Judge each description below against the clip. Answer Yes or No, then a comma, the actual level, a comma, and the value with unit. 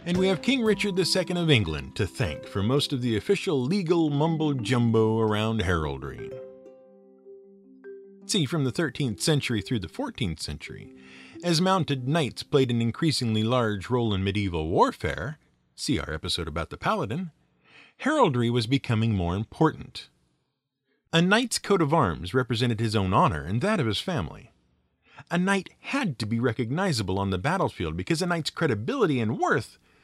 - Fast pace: No, average, 160 wpm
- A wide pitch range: Yes, wide, 7.9 semitones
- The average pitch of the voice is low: Yes, low, 130 Hz